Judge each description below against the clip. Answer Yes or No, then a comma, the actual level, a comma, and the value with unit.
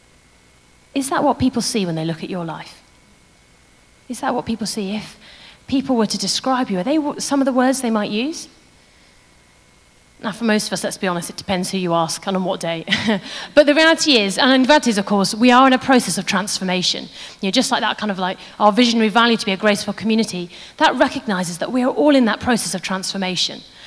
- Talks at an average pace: No, fast, 230 wpm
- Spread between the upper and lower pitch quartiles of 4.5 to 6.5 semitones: Yes, average, 5.2 semitones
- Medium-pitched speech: No, high, 215 Hz